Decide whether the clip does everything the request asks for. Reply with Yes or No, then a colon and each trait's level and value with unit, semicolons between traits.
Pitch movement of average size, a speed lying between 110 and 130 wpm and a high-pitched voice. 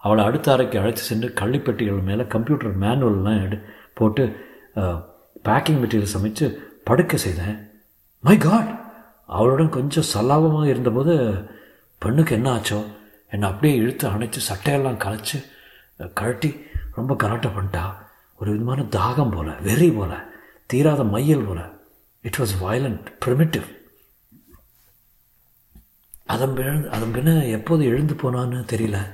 No: average, 4.8 semitones; average, 115 wpm; low, 120 Hz